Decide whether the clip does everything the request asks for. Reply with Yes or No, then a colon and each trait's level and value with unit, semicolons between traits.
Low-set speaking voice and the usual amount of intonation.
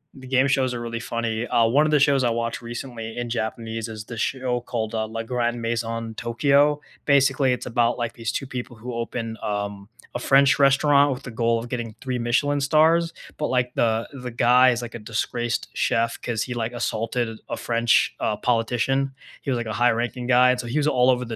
No: low, 120 Hz; narrow, 2.2 semitones